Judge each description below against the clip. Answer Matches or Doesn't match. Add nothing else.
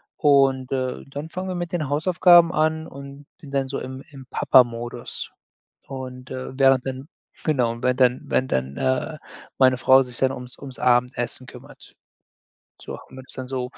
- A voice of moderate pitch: Doesn't match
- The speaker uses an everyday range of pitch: Doesn't match